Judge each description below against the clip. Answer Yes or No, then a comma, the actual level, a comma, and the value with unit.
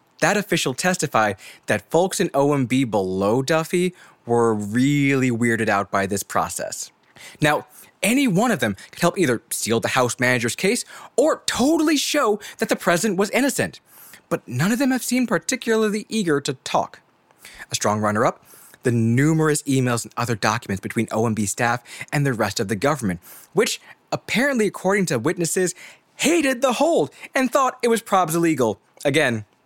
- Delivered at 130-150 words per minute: No, average, 160 wpm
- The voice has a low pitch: No, medium, 155 Hz